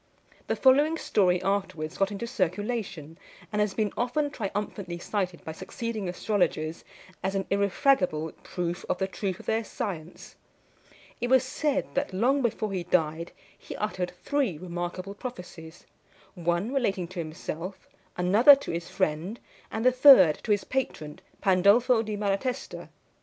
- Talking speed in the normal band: Yes, average, 145 wpm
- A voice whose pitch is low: No, high, 195 Hz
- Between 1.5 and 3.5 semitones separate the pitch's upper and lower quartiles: No, average, 4.9 semitones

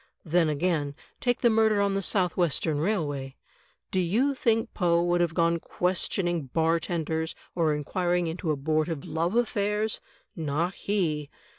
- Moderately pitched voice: Yes, medium, 170 Hz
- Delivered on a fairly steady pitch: No, average, 3.7 semitones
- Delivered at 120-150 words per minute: Yes, average, 140 wpm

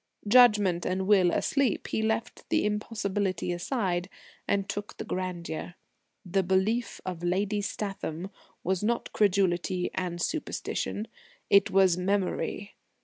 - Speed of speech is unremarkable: No, slow, 120 wpm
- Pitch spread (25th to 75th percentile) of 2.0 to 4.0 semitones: Yes, narrow, 2.5 semitones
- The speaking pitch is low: No, high, 195 Hz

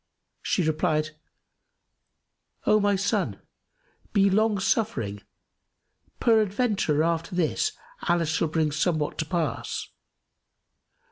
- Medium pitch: Yes, medium, 175 Hz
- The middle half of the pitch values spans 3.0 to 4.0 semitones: No, average, 4.7 semitones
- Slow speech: Yes, slow, 90 wpm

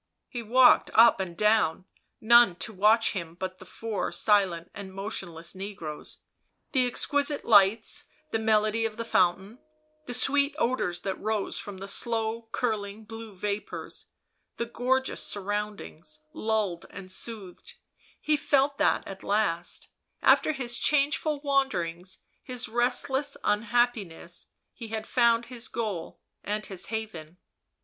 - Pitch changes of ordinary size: Yes, average, 3.9 semitones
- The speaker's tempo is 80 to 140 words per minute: Yes, slow, 135 wpm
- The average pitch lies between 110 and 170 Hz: No, high, 220 Hz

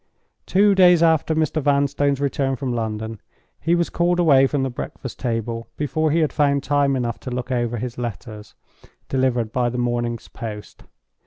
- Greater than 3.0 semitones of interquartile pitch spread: Yes, average, 3.7 semitones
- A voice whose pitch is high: No, low, 135 Hz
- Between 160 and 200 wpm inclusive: Yes, average, 170 wpm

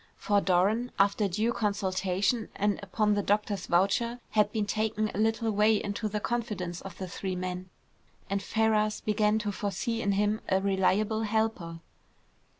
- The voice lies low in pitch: No, high, 205 Hz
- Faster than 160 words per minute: No, average, 155 wpm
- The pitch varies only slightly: Yes, narrow, 2.1 semitones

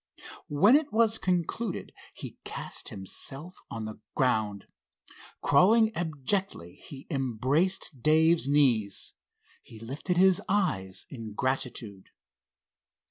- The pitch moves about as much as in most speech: No, wide, 8.5 semitones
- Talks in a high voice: No, medium, 145 Hz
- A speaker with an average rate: No, slow, 100 wpm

